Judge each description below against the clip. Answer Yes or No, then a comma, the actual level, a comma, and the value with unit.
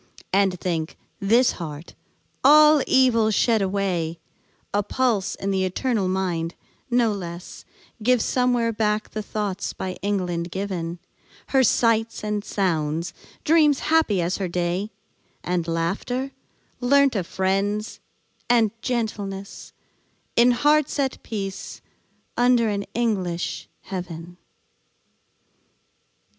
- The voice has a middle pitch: No, high, 200 Hz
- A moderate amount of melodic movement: Yes, average, 4.8 semitones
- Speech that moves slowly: Yes, slow, 110 wpm